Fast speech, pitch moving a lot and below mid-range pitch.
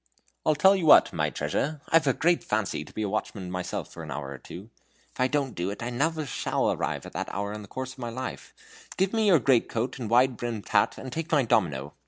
Yes: fast, 260 wpm; wide, 6.4 semitones; low, 120 Hz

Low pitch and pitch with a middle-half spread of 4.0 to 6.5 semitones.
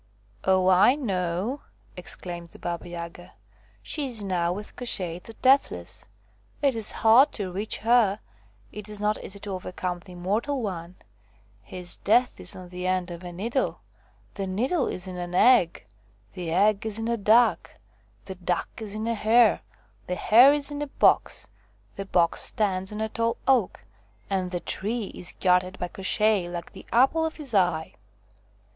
No: high, 195 Hz; average, 4.3 semitones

